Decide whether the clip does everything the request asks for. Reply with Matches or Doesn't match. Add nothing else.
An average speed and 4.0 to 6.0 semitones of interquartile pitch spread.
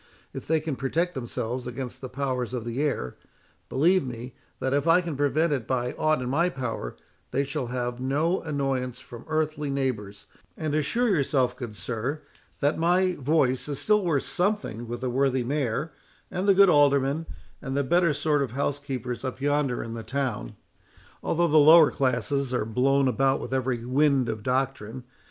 Doesn't match